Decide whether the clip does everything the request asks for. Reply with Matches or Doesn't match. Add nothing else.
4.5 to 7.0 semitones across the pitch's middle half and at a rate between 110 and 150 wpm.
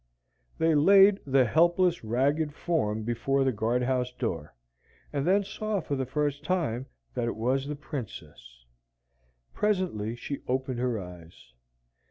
Matches